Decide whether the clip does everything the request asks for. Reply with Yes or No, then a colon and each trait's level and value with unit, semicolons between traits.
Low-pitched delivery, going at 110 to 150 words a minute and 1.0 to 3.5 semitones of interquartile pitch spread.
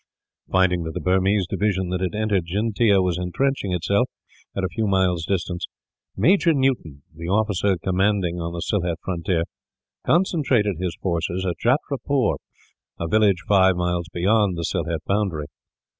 Yes: very low, 95 Hz; average, 145 wpm; average, 3.2 semitones